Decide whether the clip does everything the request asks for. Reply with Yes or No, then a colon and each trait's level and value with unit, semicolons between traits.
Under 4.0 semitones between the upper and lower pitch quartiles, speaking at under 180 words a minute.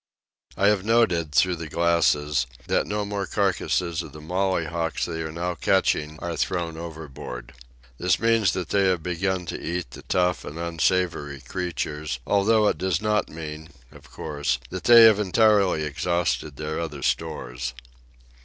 Yes: average, 3.6 semitones; average, 155 wpm